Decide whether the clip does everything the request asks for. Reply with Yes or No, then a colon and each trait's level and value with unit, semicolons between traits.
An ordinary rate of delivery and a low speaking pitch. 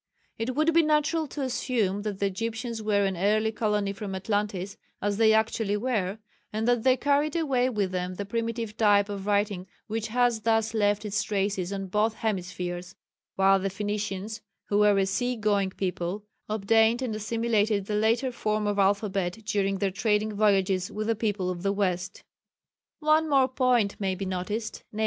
No: average, 175 wpm; high, 210 Hz